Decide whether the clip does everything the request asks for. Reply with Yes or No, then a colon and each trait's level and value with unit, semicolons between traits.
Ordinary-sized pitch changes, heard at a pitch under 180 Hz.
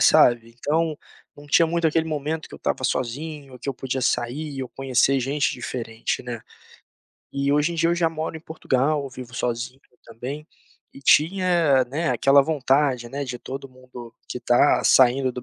Yes: average, 3.5 semitones; low, 135 Hz